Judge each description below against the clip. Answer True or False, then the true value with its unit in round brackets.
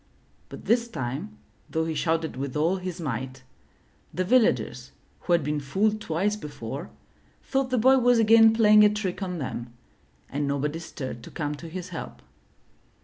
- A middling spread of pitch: False (6.9 semitones)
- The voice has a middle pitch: True (170 Hz)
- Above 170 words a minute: False (165 wpm)